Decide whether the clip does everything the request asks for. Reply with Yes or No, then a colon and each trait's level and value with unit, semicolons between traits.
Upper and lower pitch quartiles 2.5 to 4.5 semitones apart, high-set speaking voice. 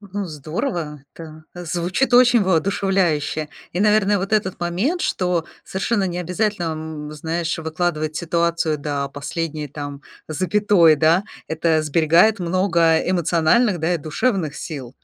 No: average, 3.5 semitones; medium, 170 Hz